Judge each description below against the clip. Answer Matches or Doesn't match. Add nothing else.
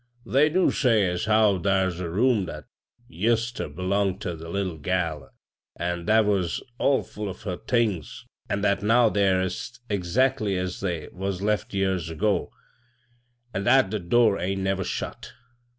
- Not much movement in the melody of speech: Doesn't match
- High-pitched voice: Doesn't match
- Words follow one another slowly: Doesn't match